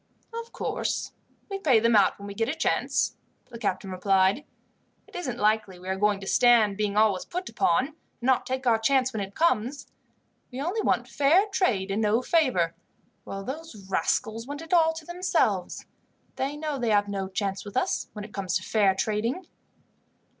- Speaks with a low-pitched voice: No, high, 225 Hz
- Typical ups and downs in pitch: No, wide, 6.5 semitones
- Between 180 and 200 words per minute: Yes, average, 190 wpm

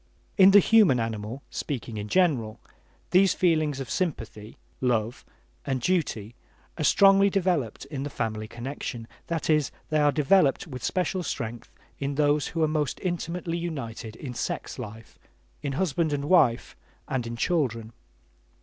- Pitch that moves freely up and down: Yes, wide, 6.5 semitones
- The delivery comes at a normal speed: Yes, average, 150 wpm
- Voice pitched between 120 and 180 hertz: Yes, medium, 140 Hz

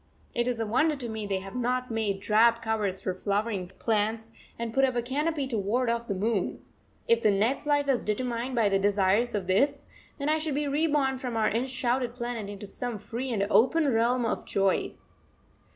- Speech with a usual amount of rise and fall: Yes, average, 3.8 semitones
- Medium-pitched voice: No, high, 235 Hz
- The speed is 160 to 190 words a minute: No, average, 200 wpm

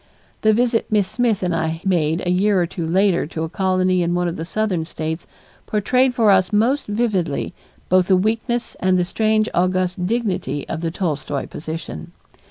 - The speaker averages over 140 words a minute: Yes, average, 180 wpm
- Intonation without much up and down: No, average, 4.2 semitones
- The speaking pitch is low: No, medium, 185 Hz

